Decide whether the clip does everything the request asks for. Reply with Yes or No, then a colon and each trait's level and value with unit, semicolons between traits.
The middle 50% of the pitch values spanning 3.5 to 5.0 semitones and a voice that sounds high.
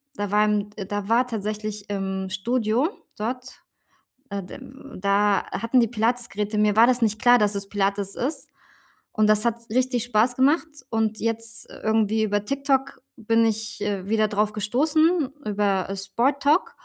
No: average, 2.9 semitones; high, 215 Hz